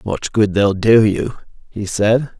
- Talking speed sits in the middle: Yes, average, 175 wpm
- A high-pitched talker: No, low, 105 Hz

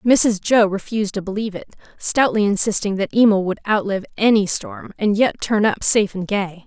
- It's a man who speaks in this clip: No, female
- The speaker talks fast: No, average, 190 wpm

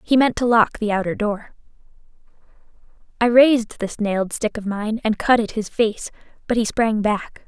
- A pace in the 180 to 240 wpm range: Yes, average, 185 wpm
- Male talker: No, female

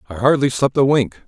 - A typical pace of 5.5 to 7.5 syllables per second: Yes, 5.7 syllables/s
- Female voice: No, male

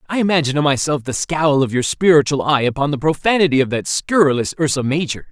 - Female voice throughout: No, male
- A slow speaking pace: No, fast, 205 wpm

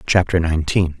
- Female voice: No, male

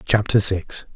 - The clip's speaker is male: Yes, male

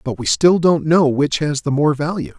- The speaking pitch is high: No, medium, 150 Hz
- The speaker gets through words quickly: Yes, fast, 250 wpm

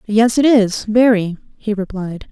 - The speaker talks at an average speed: Yes, average, 155 wpm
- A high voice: Yes, high, 215 Hz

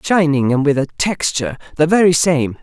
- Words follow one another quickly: No, average, 160 wpm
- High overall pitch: No, medium, 150 Hz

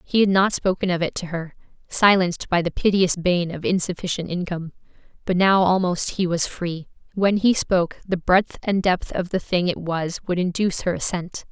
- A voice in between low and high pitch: Yes, medium, 180 Hz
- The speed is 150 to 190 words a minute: No, average, 200 wpm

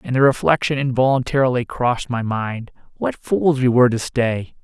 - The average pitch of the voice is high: No, low, 125 Hz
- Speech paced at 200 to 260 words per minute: No, average, 155 wpm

